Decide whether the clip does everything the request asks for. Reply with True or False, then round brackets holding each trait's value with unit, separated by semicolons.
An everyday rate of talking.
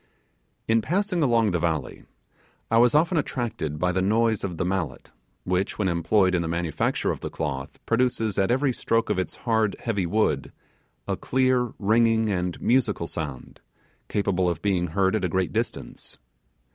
True (170 wpm)